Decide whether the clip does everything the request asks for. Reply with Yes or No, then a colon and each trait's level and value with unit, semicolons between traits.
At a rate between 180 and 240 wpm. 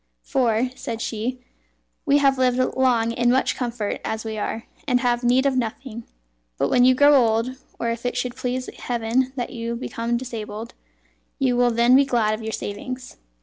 Yes: average, 185 wpm